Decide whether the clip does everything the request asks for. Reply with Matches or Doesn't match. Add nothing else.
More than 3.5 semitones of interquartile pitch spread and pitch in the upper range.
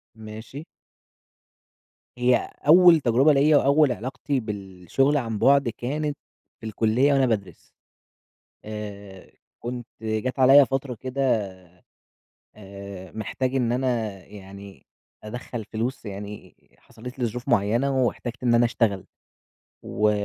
Doesn't match